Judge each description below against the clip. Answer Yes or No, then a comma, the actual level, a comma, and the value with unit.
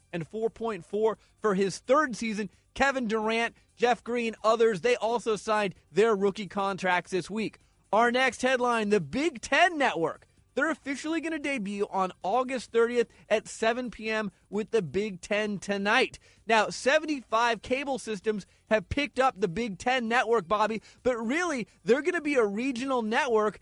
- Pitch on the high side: Yes, high, 225 Hz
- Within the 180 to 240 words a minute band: No, average, 160 wpm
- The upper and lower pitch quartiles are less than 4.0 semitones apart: Yes, average, 3.3 semitones